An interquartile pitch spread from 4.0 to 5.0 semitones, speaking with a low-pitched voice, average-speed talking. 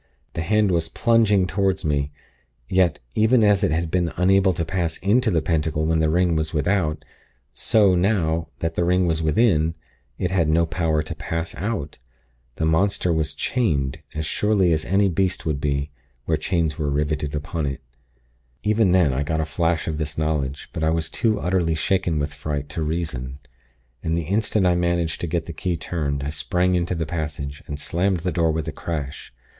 No: average, 3.1 semitones; very low, 80 Hz; average, 190 wpm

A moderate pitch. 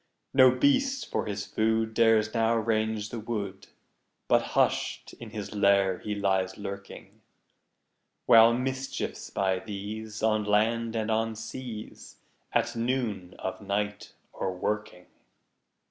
No: low, 110 Hz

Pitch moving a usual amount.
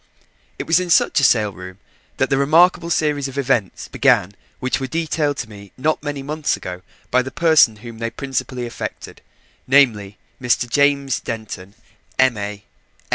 Yes: average, 4.6 semitones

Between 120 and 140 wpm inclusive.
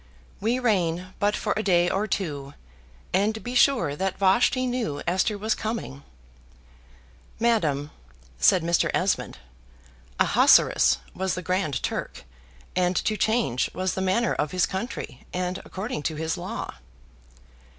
Yes: slow, 135 wpm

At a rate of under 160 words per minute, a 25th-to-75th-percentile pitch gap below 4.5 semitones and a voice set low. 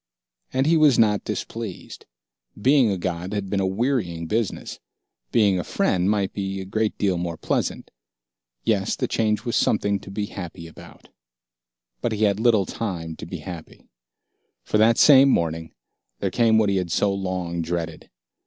No: average, 170 wpm; average, 3.7 semitones; low, 100 Hz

